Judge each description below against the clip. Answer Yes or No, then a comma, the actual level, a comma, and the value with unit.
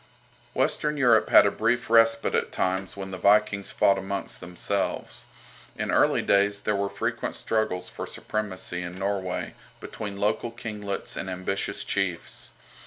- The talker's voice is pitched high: No, low, 100 Hz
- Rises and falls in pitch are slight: Yes, narrow, 2.2 semitones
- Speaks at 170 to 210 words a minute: No, average, 145 wpm